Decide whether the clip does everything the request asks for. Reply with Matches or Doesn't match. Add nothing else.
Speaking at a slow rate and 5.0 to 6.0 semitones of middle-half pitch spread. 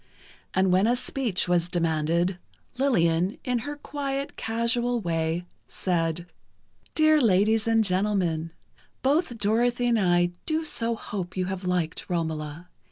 Matches